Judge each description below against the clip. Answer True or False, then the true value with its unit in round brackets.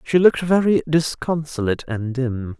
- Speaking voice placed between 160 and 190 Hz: False (145 Hz)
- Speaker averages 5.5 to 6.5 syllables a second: False (5.0 syllables/s)